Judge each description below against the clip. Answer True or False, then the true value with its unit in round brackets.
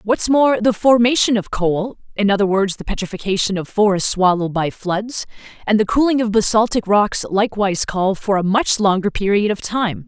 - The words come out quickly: False (185 wpm)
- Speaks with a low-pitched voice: False (205 Hz)